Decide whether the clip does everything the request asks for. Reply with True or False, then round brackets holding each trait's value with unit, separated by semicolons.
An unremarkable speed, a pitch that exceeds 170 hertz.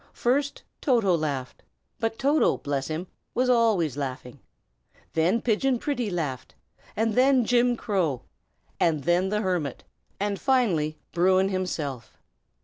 False (130 wpm; 190 Hz)